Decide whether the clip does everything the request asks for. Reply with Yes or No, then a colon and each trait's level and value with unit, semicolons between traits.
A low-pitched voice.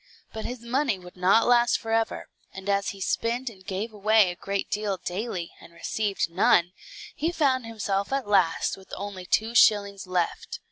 No: high, 205 Hz